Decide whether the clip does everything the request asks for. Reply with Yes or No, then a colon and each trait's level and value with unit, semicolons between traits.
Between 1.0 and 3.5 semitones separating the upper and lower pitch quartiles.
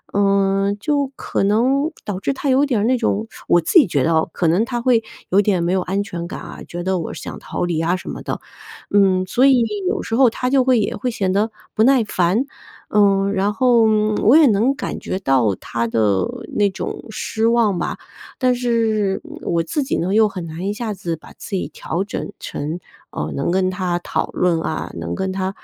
No: average, 5.0 semitones